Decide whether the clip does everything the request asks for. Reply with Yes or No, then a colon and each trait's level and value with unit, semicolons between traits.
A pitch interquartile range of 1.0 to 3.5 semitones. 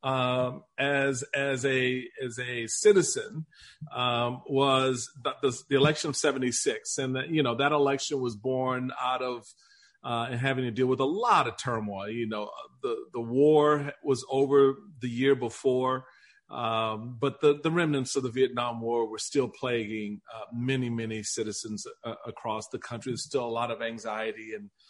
Yes: average, 2.8 semitones